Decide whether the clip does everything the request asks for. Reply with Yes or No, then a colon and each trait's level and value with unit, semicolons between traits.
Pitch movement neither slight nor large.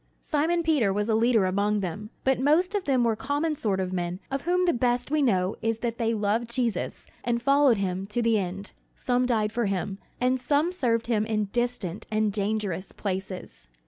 Yes: average, 4.3 semitones